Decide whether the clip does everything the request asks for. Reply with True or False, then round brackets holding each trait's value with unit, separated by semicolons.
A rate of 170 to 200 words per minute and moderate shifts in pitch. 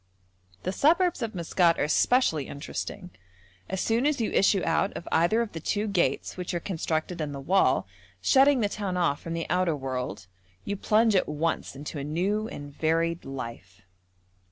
False (180 wpm; 5.7 semitones)